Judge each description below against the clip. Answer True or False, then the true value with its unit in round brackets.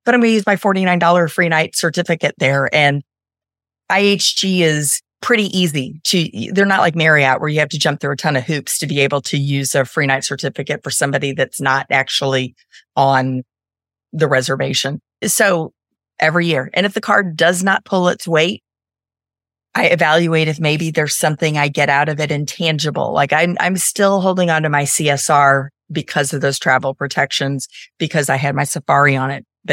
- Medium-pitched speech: True (150 Hz)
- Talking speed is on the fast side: False (190 wpm)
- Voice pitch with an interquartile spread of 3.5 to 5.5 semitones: True (3.9 semitones)